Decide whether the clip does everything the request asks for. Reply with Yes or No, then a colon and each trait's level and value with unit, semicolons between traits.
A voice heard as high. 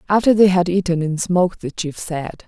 No: medium, 175 Hz